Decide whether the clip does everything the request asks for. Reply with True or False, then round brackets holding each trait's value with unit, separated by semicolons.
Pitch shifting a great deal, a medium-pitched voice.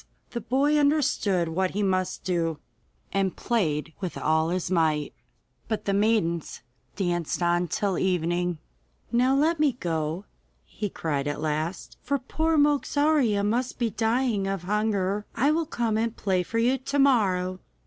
False (6.0 semitones; 200 Hz)